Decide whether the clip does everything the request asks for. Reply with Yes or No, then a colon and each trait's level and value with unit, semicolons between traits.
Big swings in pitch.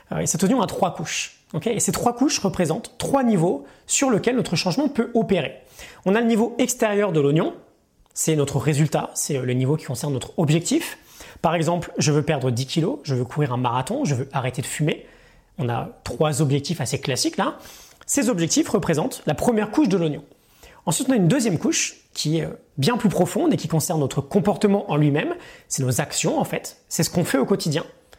Yes: wide, 6.1 semitones